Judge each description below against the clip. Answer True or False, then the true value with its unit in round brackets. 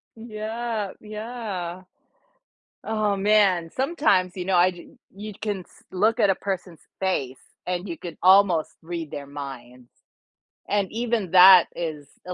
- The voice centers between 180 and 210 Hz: True (190 Hz)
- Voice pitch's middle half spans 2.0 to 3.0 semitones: False (3.8 semitones)